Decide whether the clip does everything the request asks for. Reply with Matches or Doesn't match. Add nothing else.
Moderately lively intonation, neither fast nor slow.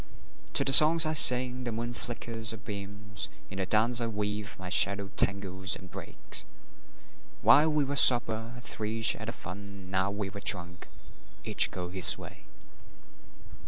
Matches